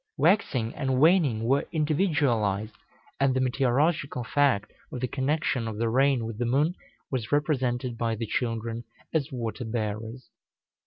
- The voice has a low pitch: Yes, low, 125 Hz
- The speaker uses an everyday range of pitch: Yes, average, 3.8 semitones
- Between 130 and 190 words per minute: Yes, average, 145 wpm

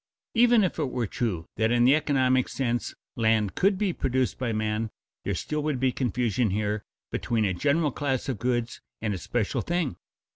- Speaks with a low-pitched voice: Yes, low, 125 Hz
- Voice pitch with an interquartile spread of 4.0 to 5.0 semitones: Yes, average, 4.5 semitones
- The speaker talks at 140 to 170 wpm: No, average, 185 wpm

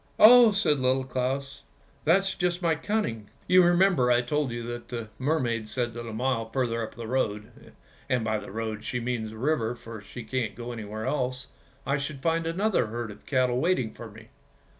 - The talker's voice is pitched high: No, low, 125 Hz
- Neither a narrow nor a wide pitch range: Yes, average, 4.8 semitones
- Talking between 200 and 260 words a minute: Yes, fast, 205 wpm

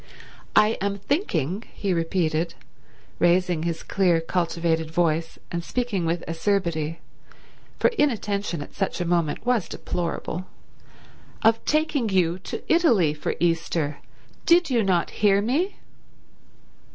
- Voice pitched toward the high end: No, medium, 180 Hz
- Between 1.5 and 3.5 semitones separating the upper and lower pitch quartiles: No, average, 4.3 semitones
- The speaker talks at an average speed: No, slow, 120 wpm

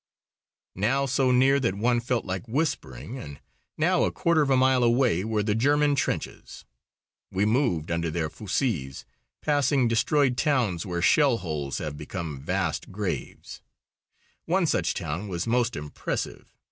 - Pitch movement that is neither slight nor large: No, wide, 7.4 semitones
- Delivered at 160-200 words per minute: No, average, 145 wpm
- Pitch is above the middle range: No, low, 115 Hz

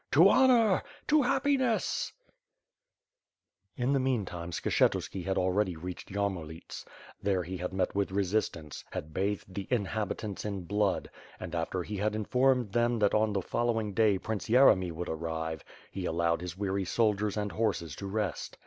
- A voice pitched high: No, low, 100 Hz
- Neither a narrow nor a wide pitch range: Yes, average, 3.6 semitones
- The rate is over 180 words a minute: No, average, 165 wpm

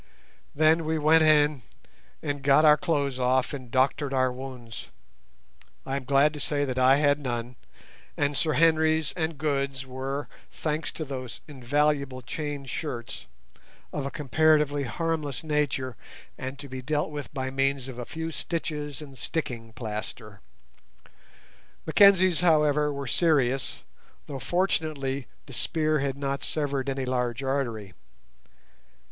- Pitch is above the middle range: No, medium, 140 Hz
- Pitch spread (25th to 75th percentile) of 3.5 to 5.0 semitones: No, average, 2.8 semitones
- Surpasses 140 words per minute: No, slow, 135 wpm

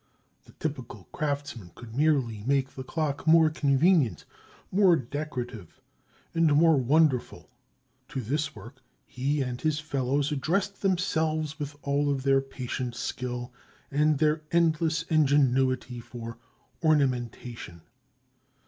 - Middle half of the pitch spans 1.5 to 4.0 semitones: Yes, average, 3.7 semitones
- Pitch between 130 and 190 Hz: Yes, medium, 140 Hz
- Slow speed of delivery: Yes, slow, 115 wpm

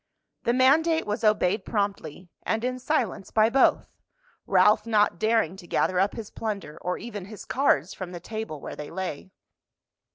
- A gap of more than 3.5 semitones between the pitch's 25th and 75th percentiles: Yes, average, 3.9 semitones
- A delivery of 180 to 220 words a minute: No, average, 165 wpm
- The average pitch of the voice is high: Yes, high, 210 Hz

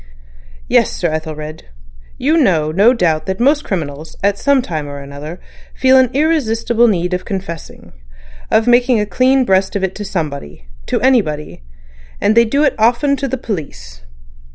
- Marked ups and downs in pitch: Yes, wide, 8.1 semitones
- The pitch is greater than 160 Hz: Yes, high, 190 Hz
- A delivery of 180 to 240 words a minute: No, average, 155 wpm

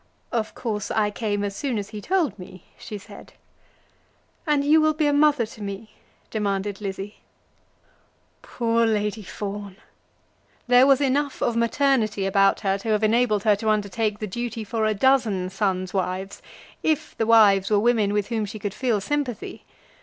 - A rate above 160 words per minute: Yes, average, 170 wpm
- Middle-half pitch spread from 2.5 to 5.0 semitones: Yes, average, 3.2 semitones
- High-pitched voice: Yes, high, 215 Hz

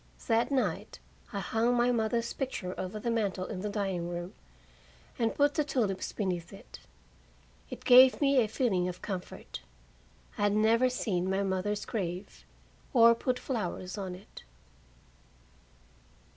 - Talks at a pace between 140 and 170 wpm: Yes, average, 145 wpm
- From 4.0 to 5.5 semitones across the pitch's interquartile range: Yes, average, 4.3 semitones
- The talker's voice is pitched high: Yes, high, 210 Hz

